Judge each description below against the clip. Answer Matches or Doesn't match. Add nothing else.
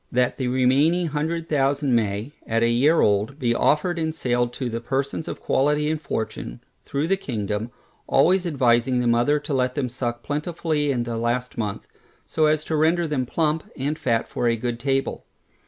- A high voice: Doesn't match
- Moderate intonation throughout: Matches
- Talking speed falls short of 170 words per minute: Doesn't match